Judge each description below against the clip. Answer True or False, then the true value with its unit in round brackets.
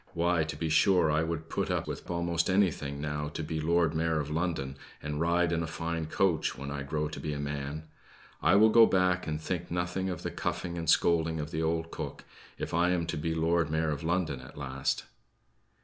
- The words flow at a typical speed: False (220 wpm)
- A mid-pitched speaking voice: False (80 Hz)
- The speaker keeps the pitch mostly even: True (2.2 semitones)